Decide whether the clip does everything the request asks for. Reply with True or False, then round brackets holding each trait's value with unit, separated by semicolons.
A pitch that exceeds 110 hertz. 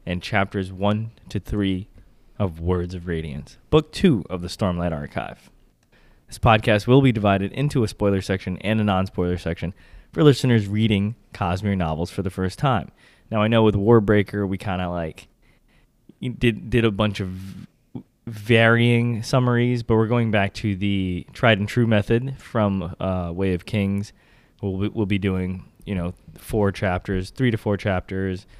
False (100 Hz)